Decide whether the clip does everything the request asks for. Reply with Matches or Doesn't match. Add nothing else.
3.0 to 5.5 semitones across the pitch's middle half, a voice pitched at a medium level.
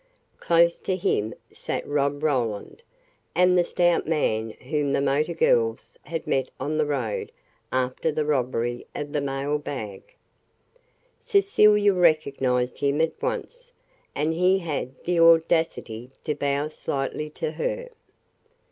Matches